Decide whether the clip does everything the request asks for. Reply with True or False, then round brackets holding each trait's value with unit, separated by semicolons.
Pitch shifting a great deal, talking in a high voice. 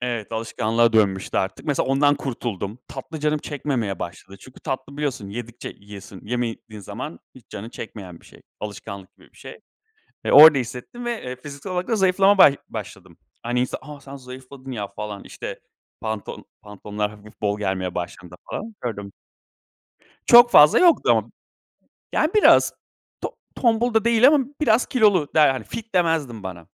False (7.1 semitones; 125 Hz)